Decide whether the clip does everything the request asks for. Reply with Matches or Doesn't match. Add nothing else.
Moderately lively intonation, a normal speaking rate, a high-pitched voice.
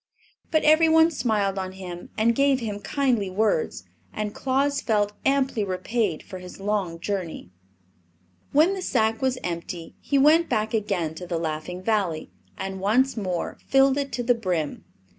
Doesn't match